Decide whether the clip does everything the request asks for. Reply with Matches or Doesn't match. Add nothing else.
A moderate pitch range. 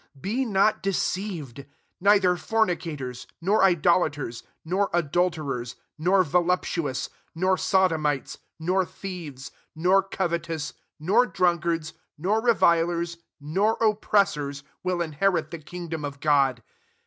Matches